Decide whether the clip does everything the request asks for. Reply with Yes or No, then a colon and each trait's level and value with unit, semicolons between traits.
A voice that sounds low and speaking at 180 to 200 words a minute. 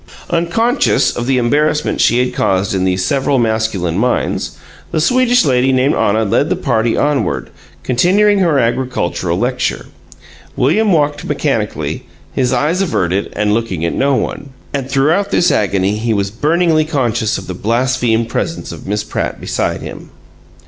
No: low, 125 Hz; average, 155 wpm